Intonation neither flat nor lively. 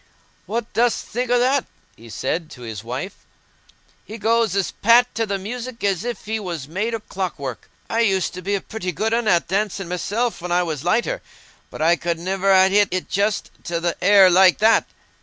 Yes: average, 4.4 semitones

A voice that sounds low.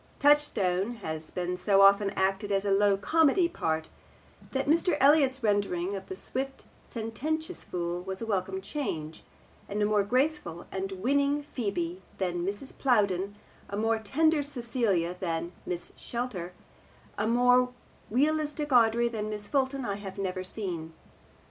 No: high, 205 Hz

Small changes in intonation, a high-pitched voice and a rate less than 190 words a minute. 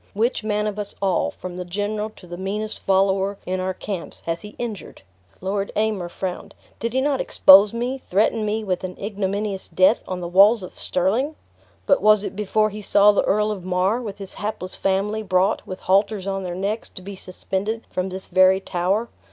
No: narrow, 2.2 semitones; high, 200 Hz; average, 200 wpm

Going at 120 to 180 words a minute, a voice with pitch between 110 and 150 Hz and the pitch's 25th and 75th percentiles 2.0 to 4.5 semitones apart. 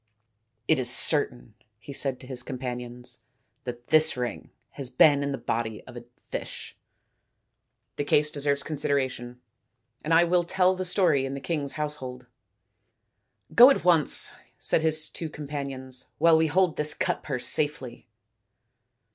Yes: average, 160 wpm; medium, 140 Hz; average, 3.8 semitones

